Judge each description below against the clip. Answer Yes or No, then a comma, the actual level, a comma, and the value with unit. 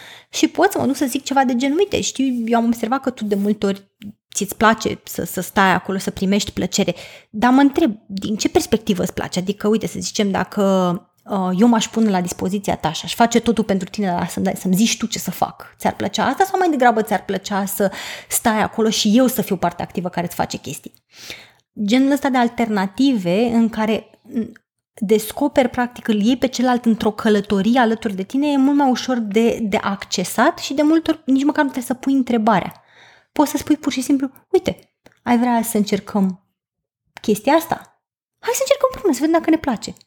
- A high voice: Yes, high, 225 Hz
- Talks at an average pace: No, fast, 215 wpm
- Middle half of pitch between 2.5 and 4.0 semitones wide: No, average, 5.0 semitones